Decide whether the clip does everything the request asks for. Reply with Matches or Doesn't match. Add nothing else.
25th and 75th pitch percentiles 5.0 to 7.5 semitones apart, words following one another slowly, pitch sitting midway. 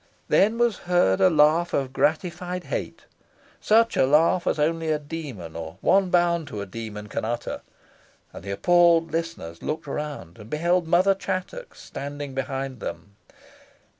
Doesn't match